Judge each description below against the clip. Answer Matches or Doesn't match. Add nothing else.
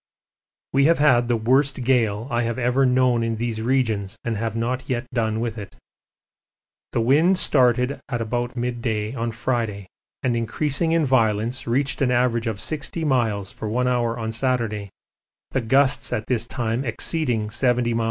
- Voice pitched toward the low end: Matches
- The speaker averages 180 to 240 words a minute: Doesn't match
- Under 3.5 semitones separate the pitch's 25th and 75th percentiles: Matches